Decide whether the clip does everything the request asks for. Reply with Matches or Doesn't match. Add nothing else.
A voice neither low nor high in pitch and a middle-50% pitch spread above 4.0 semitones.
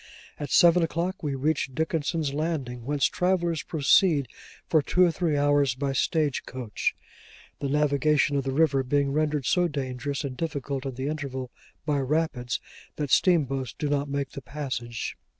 Doesn't match